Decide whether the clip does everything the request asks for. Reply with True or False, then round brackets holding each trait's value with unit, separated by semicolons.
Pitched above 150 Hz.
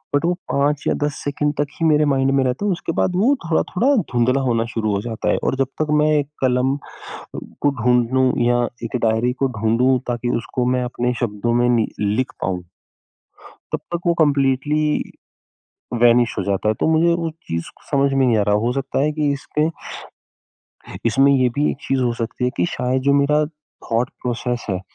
False (130 Hz)